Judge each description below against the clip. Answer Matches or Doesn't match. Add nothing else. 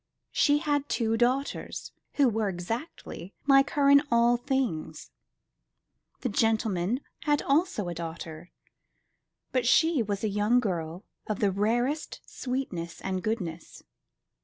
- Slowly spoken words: Matches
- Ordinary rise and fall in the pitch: Doesn't match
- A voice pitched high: Matches